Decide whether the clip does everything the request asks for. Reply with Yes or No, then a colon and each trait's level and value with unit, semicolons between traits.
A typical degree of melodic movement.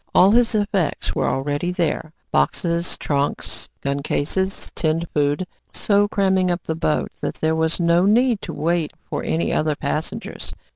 Yes: average, 3.8 semitones